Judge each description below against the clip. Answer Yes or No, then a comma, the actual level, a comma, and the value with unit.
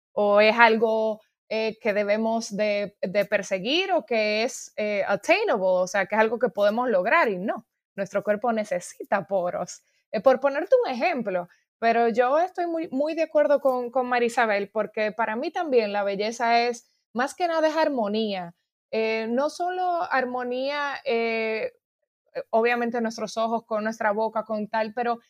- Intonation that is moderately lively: Yes, average, 3.8 semitones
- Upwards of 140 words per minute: Yes, average, 165 wpm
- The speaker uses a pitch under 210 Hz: No, high, 230 Hz